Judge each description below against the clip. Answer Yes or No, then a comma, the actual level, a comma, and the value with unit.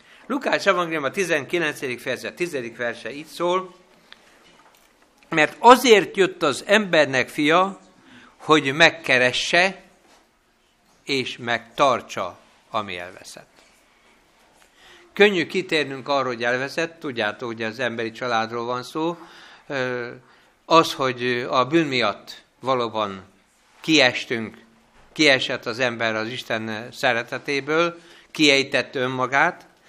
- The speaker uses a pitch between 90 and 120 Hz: No, low, 135 Hz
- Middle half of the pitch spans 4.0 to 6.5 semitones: Yes, wide, 5.6 semitones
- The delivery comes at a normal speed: No, slow, 100 wpm